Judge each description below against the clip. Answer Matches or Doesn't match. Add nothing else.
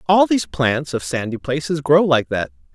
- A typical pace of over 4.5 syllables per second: Matches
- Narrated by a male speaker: Matches